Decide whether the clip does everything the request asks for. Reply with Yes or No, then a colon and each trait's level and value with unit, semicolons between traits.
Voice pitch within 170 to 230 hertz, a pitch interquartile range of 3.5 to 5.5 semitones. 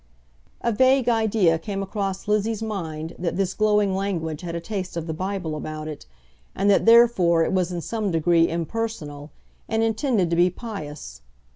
Yes: high, 190 Hz; average, 4.6 semitones